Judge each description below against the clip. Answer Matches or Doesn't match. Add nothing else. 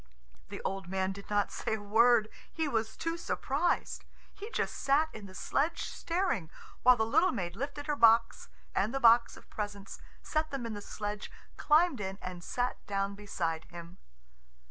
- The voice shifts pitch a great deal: Matches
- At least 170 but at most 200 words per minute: Matches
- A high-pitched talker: Matches